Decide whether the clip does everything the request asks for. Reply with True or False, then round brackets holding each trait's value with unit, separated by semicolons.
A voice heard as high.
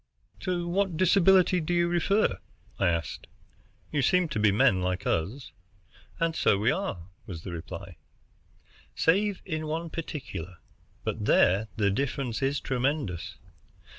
False (140 Hz)